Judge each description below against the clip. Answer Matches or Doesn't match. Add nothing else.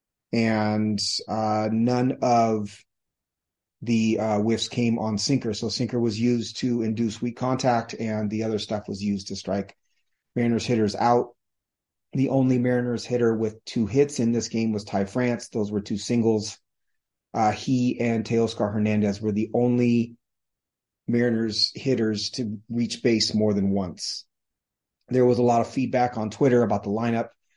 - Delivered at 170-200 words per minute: Doesn't match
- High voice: Doesn't match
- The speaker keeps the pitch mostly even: Matches